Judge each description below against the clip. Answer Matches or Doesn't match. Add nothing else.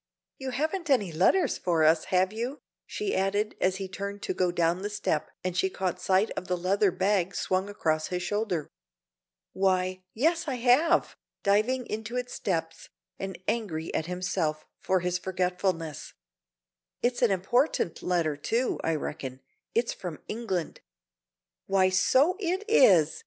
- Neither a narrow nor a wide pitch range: Matches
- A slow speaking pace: Doesn't match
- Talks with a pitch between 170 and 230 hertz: Matches